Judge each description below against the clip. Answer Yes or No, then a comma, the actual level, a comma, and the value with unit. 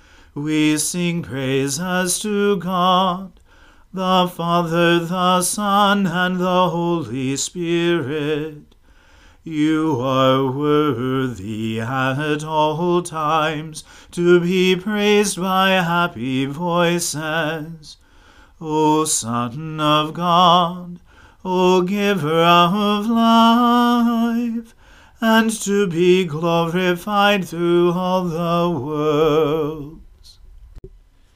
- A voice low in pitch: No, medium, 170 Hz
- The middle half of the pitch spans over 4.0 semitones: No, average, 3.3 semitones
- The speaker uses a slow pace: Yes, slow, 80 wpm